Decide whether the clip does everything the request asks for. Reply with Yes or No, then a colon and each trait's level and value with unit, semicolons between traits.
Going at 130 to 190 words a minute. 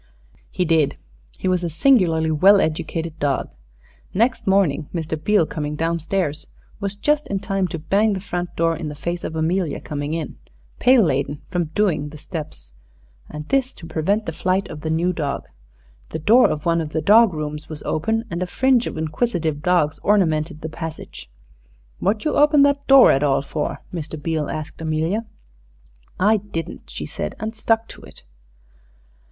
Yes: average, 180 wpm